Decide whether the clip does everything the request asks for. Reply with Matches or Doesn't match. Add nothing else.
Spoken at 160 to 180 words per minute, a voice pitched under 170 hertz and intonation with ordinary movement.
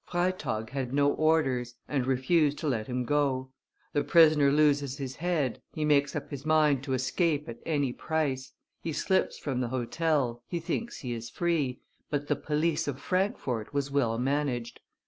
Matches